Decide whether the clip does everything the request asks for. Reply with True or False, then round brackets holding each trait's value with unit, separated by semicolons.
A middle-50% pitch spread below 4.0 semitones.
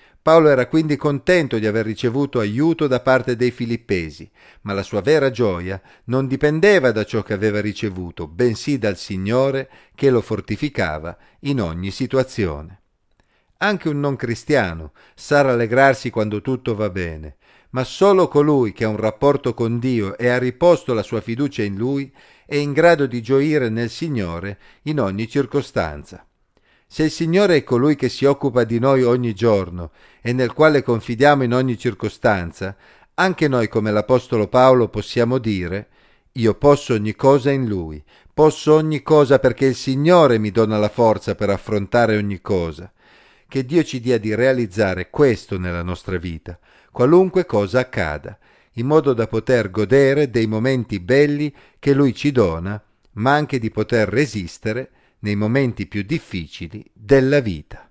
False (4.9 semitones)